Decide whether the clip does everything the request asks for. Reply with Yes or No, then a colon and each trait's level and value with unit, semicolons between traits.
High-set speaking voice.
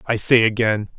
No: low, 110 Hz